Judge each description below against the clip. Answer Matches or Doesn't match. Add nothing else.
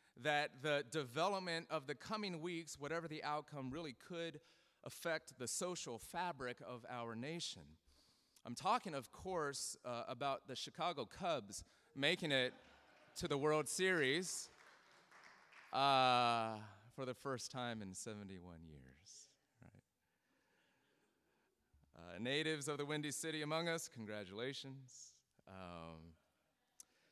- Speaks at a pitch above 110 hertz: Matches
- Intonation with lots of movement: Matches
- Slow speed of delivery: Matches